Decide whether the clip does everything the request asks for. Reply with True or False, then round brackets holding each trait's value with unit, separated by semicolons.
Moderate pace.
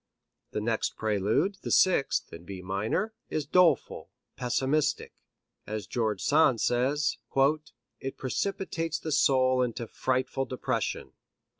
False (115 wpm)